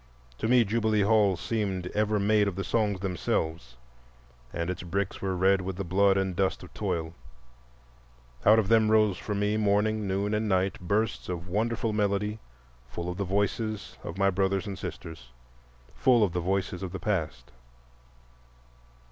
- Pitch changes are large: No, narrow, 2.5 semitones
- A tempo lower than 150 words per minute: No, average, 165 wpm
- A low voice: Yes, low, 100 Hz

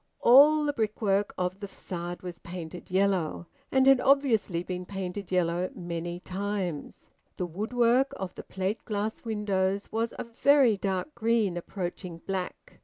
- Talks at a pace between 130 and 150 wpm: Yes, average, 145 wpm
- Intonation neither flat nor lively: Yes, average, 4.1 semitones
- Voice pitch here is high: Yes, high, 195 Hz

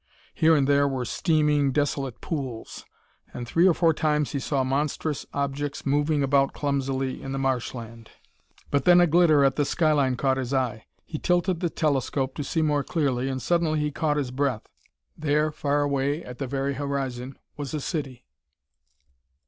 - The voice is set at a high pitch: No, medium, 140 Hz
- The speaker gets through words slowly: No, average, 175 wpm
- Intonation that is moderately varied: No, narrow, 2.2 semitones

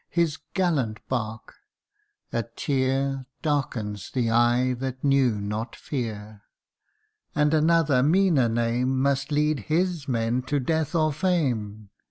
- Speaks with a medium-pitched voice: No, low, 130 Hz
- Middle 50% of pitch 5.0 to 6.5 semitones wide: No, average, 4.5 semitones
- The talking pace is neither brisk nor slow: No, slow, 120 wpm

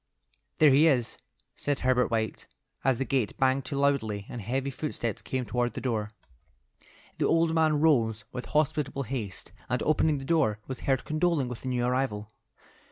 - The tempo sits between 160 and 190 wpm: Yes, average, 170 wpm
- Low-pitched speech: Yes, low, 130 Hz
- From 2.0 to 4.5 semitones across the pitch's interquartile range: Yes, average, 3.4 semitones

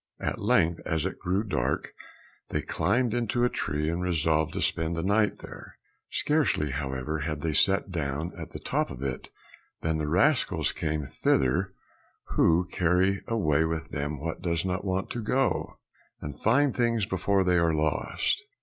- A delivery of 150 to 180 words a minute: Yes, average, 165 wpm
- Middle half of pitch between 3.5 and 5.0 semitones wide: Yes, average, 4.3 semitones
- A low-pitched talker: Yes, very low, 85 Hz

